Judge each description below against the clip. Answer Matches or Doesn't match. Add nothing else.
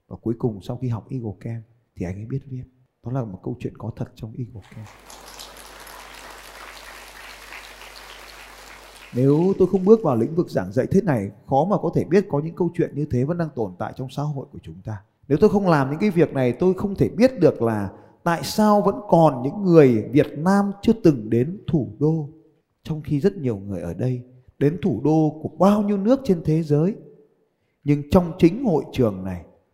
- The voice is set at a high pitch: Doesn't match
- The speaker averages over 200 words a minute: Matches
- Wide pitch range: Matches